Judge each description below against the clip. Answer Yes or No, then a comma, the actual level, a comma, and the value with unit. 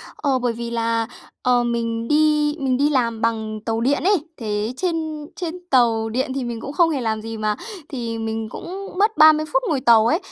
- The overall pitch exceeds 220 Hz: Yes, high, 245 Hz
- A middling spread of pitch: Yes, average, 5.0 semitones